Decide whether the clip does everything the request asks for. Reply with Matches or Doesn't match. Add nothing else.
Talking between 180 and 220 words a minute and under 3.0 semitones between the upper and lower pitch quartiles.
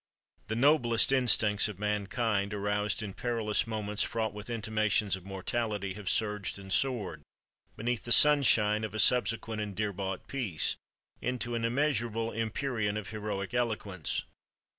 Doesn't match